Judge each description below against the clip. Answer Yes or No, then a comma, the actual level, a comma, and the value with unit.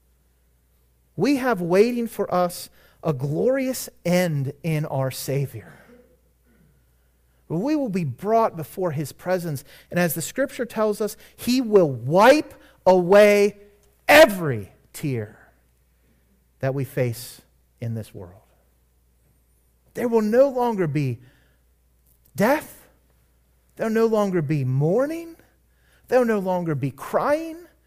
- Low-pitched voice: No, medium, 150 Hz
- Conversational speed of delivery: No, slow, 115 wpm